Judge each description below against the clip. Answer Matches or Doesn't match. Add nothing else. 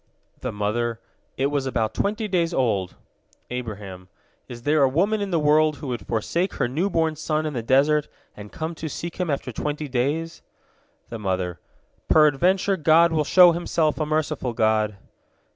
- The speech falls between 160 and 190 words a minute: Matches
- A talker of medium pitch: Matches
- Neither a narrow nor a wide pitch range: Doesn't match